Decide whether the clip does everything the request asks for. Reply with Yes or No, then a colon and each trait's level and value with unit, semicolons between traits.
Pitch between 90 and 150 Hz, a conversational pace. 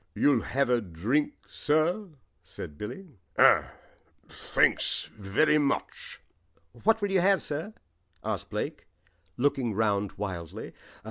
No: medium, 140 Hz; slow, 115 wpm